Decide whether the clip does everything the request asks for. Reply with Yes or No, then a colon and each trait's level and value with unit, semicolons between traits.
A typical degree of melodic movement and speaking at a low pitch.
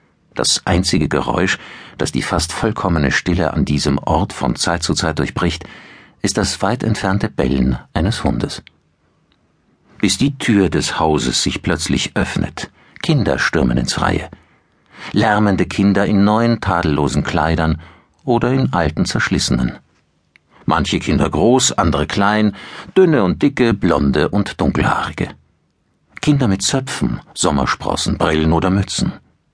Yes: average, 4.8 semitones; very low, 95 Hz